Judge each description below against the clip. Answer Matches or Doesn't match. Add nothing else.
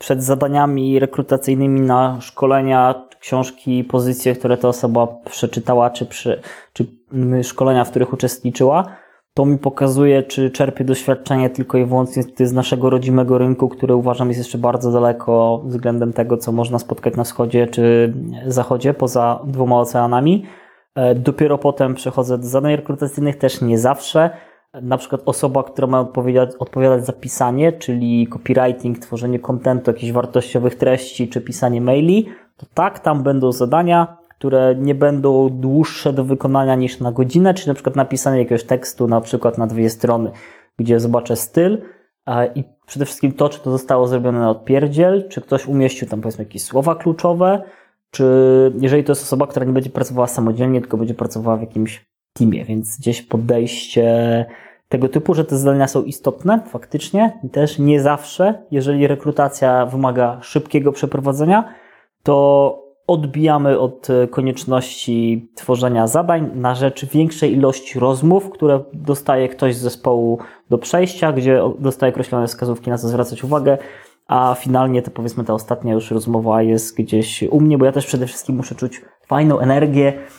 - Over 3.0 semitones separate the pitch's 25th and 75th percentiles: Doesn't match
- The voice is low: Matches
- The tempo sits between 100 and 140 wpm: Doesn't match